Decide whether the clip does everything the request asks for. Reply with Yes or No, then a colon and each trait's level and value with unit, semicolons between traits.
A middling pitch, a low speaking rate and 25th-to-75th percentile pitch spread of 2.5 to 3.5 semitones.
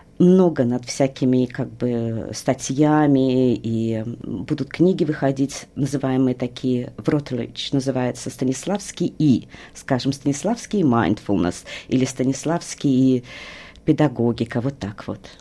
No: low, 130 Hz; slow, 105 wpm; average, 2.9 semitones